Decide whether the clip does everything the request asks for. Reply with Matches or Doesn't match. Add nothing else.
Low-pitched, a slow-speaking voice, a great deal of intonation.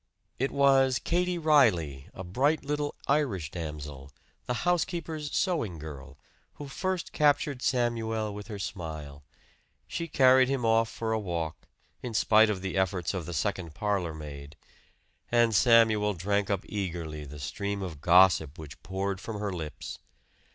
Doesn't match